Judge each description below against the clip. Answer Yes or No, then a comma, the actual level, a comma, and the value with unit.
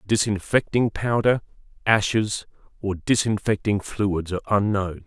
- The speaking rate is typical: No, slow, 95 wpm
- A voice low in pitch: Yes, low, 105 Hz